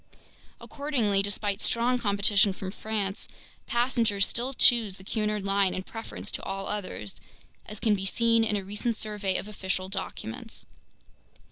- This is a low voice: No, high, 205 Hz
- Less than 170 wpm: Yes, average, 145 wpm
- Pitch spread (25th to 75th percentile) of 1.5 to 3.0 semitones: Yes, narrow, 2.5 semitones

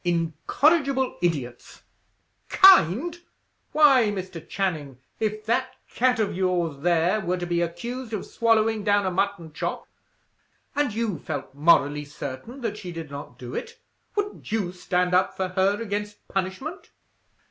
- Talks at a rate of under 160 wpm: Yes, average, 140 wpm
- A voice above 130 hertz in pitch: Yes, high, 190 Hz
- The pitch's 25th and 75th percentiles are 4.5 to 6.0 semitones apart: Yes, average, 5.2 semitones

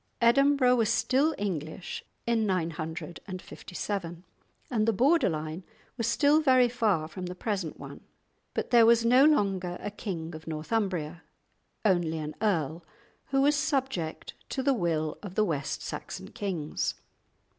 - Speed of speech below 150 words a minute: Yes, average, 140 wpm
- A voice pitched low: No, high, 195 Hz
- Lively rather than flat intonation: Yes, wide, 6.6 semitones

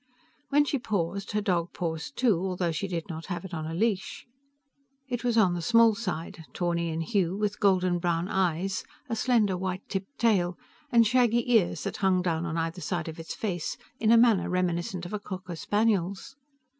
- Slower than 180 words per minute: No, average, 195 wpm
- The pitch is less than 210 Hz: Yes, medium, 185 Hz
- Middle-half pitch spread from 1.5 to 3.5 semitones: No, average, 4.0 semitones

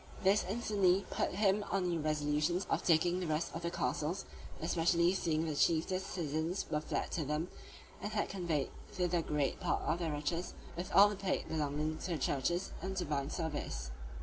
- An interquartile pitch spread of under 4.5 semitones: Yes, average, 3.3 semitones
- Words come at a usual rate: Yes, average, 180 wpm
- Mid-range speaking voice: Yes, medium, 170 Hz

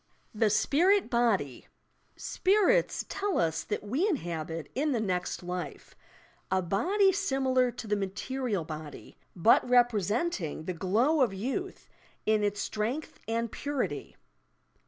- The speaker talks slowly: Yes, slow, 130 wpm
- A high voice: Yes, high, 225 Hz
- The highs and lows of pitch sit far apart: Yes, wide, 7.1 semitones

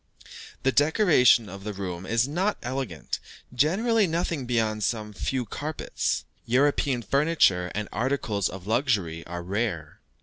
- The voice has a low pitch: Yes, low, 120 Hz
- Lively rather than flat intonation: Yes, wide, 6.5 semitones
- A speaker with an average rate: No, slow, 130 wpm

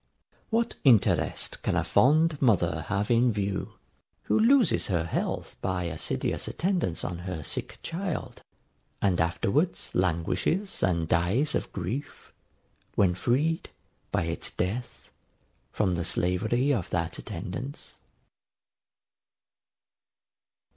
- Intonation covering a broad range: Yes, wide, 8.5 semitones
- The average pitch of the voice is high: No, low, 100 Hz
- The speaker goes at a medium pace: No, slow, 110 wpm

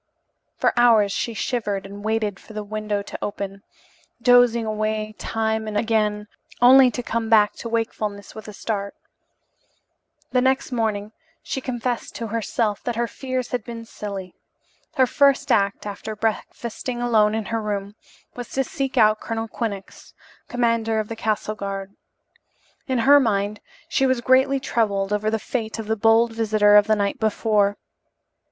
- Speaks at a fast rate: No, average, 160 wpm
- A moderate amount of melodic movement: No, narrow, 2.3 semitones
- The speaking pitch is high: Yes, high, 220 Hz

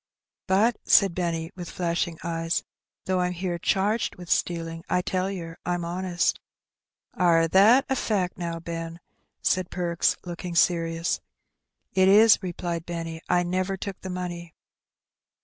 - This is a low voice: No, medium, 175 Hz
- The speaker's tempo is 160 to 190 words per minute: No, average, 140 wpm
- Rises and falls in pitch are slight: Yes, narrow, 1.9 semitones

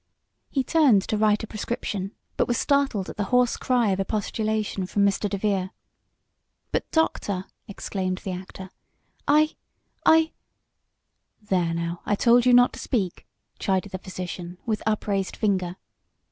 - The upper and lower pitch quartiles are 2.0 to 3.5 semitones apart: No, average, 3.9 semitones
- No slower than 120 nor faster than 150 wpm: Yes, average, 145 wpm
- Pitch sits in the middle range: No, high, 205 Hz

